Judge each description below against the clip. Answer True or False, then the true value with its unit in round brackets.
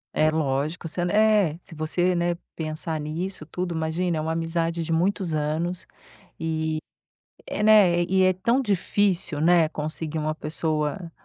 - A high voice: False (165 Hz)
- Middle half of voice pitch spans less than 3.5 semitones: True (2.6 semitones)